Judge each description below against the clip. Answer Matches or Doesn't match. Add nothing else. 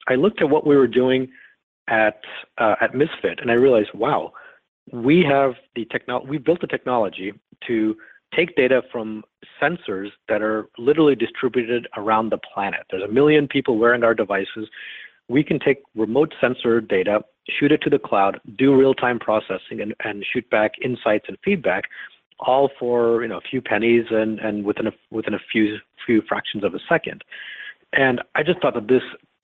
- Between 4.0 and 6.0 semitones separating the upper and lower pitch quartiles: Doesn't match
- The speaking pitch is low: Matches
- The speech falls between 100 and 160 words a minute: Doesn't match